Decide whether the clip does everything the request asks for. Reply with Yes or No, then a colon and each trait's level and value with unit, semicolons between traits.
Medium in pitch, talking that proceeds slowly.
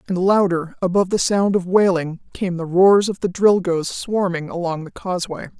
No: medium, 180 Hz; average, 180 wpm